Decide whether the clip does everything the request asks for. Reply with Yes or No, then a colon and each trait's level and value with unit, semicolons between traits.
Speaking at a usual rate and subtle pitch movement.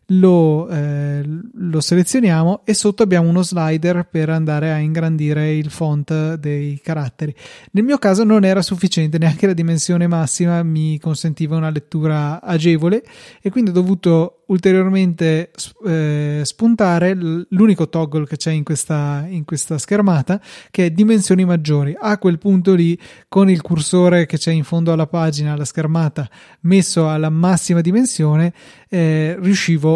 No: average, 145 wpm; average, 3.1 semitones